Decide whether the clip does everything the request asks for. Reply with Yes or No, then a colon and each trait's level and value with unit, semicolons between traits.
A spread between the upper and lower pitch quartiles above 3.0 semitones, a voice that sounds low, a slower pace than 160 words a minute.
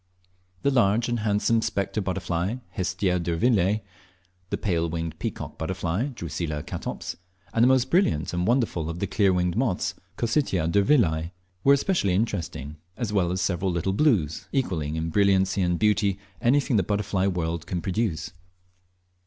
Yes: average, 4.5 semitones; very low, 95 Hz; average, 150 wpm